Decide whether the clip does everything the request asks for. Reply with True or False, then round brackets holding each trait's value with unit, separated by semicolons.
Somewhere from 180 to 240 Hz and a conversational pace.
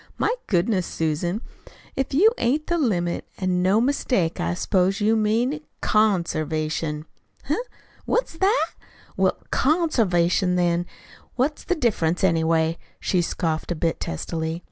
False (185 Hz; 130 wpm)